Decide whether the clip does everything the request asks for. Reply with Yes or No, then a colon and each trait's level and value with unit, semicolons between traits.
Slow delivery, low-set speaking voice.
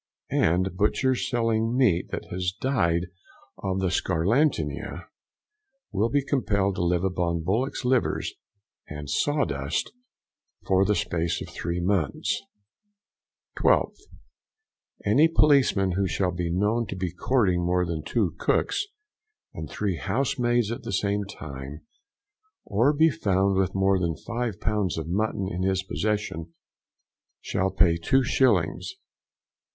Yes: slow, 125 wpm; very low, 95 Hz